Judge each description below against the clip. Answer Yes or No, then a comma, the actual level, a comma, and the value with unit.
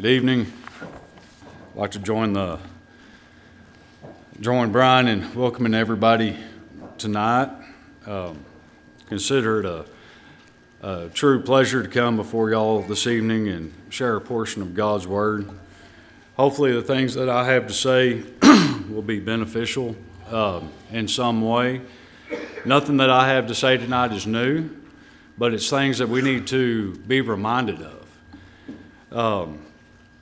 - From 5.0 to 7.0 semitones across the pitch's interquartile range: No, average, 3.8 semitones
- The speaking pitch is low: Yes, low, 115 Hz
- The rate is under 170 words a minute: Yes, slow, 135 wpm